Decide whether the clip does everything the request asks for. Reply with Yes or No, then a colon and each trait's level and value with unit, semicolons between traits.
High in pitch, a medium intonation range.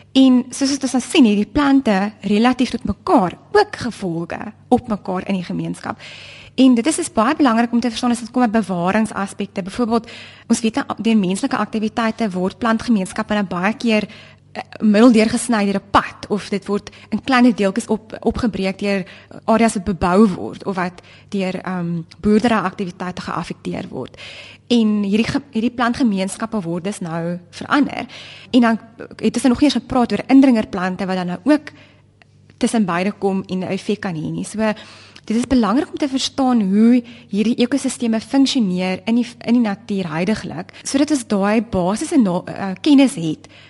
Yes: high, 220 Hz; average, 3.9 semitones